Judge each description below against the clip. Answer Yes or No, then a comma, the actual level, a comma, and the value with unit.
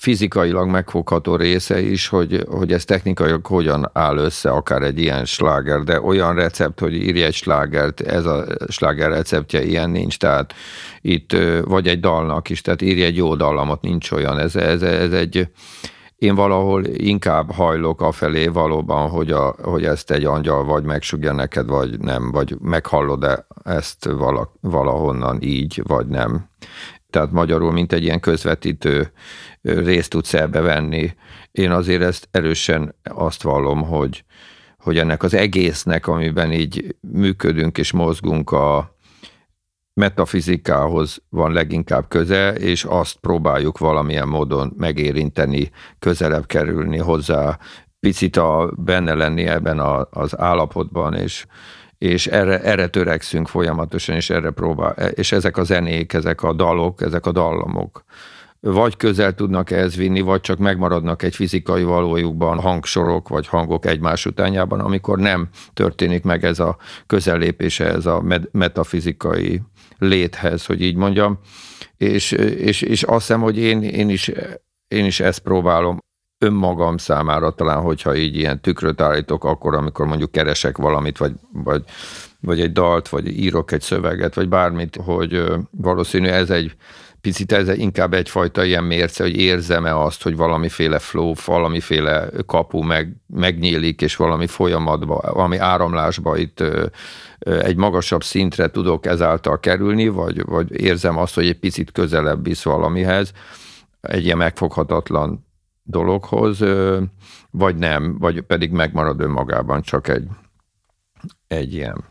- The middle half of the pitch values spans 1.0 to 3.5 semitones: Yes, average, 2.7 semitones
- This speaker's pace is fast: No, average, 140 wpm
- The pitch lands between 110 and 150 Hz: No, very low, 85 Hz